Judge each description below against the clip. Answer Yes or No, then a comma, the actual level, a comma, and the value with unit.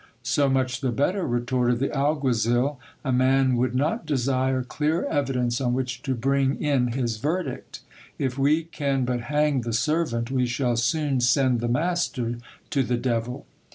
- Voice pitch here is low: Yes, low, 130 Hz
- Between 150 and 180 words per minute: Yes, average, 160 wpm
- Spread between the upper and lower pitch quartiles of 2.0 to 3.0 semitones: Yes, narrow, 2.6 semitones